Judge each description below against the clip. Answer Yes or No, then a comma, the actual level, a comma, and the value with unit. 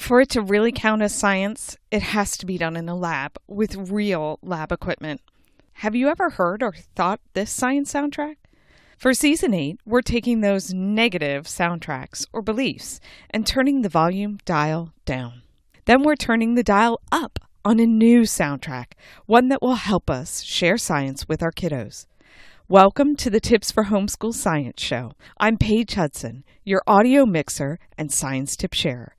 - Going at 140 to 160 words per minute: No, average, 170 wpm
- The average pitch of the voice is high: Yes, high, 200 Hz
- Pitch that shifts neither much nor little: No, wide, 6.5 semitones